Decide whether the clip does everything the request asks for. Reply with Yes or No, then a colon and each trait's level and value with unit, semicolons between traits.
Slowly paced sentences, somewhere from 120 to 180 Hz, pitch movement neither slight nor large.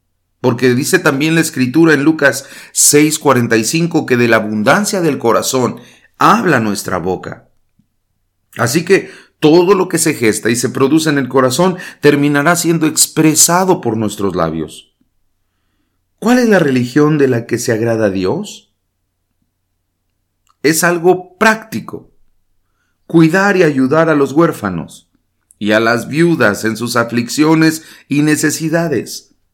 No: slow, 130 wpm; medium, 140 Hz; wide, 7.1 semitones